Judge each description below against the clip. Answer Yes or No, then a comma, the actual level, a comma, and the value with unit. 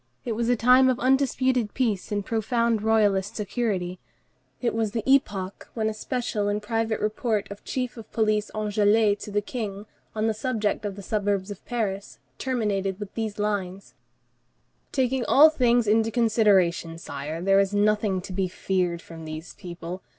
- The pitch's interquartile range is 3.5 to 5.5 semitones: No, average, 2.9 semitones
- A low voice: No, high, 210 Hz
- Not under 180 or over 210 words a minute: No, average, 165 wpm